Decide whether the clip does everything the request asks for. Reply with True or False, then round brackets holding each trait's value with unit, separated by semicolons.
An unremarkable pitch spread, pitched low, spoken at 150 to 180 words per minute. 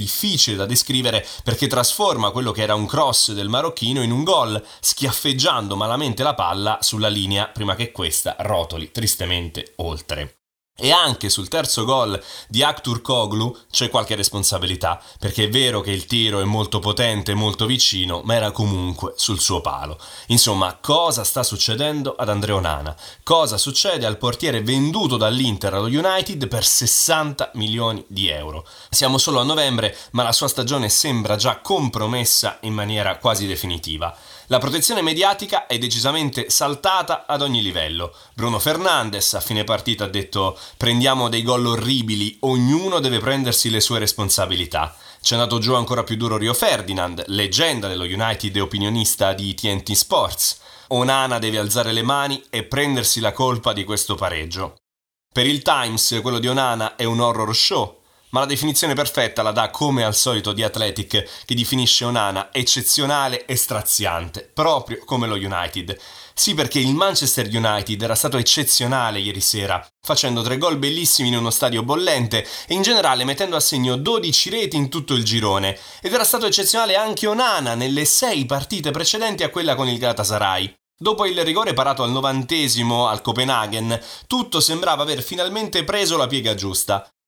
True (4.6 semitones; 115 Hz; 160 wpm)